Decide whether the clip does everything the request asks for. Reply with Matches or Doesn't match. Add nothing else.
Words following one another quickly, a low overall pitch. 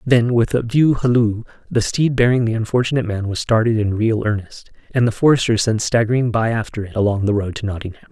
Matches